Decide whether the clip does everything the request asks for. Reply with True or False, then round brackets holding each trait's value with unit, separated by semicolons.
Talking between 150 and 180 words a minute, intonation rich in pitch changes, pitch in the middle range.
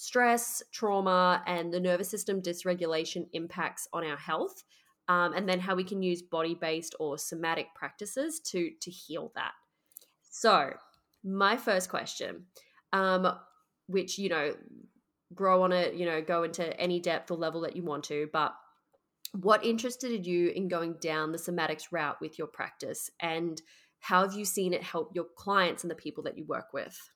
False (170 wpm; 2.8 semitones; 180 Hz)